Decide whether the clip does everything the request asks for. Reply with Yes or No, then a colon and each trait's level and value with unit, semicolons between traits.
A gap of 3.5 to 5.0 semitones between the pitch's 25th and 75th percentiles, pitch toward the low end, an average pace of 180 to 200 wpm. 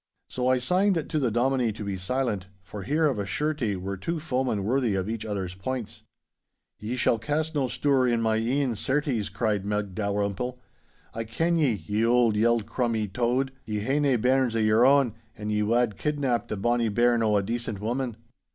Yes: average, 3.9 semitones; low, 120 Hz; average, 195 wpm